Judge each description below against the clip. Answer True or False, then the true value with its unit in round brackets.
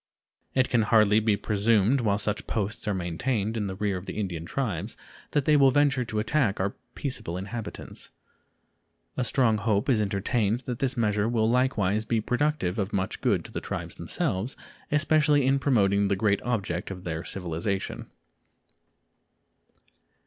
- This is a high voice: False (110 Hz)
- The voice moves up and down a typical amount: True (4.1 semitones)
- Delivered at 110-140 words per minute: False (160 wpm)